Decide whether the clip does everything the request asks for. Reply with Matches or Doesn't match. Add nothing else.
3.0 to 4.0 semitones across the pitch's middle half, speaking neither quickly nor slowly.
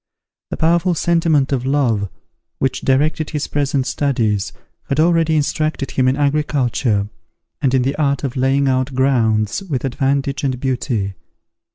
Doesn't match